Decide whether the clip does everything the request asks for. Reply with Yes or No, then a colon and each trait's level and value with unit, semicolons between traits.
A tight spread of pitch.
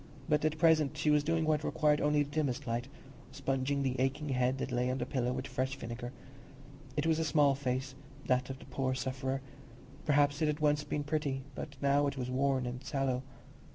Yes: narrow, 2.3 semitones